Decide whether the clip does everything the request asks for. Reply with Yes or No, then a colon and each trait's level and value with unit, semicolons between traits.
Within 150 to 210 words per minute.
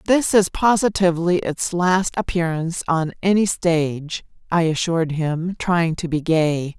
No: average, 140 wpm